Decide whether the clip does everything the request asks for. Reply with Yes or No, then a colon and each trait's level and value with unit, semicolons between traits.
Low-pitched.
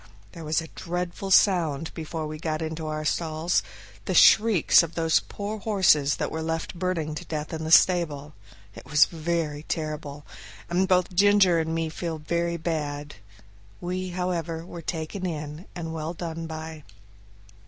No: medium, 165 Hz